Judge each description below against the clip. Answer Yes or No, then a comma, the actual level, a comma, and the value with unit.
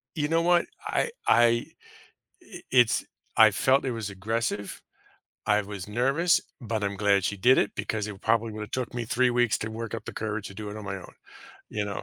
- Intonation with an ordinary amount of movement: Yes, average, 3.0 semitones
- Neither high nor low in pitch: No, low, 110 Hz